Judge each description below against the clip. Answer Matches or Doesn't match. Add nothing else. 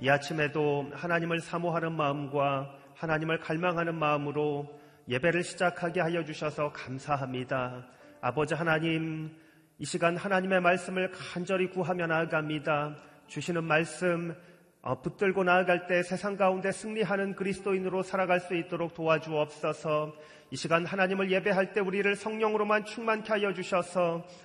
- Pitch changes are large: Doesn't match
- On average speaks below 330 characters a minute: Doesn't match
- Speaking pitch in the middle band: Matches